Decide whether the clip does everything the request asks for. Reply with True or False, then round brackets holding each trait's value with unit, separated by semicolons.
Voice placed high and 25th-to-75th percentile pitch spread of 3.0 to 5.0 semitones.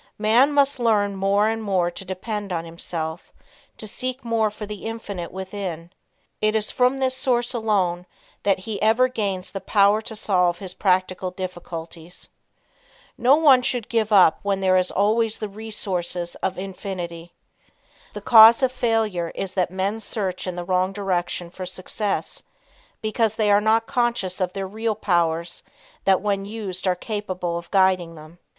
True (195 Hz; 3.3 semitones)